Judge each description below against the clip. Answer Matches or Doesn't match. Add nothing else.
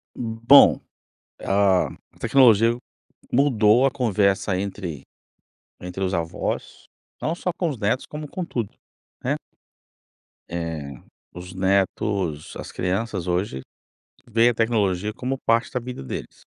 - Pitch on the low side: Matches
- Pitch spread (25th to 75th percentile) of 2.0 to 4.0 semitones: Doesn't match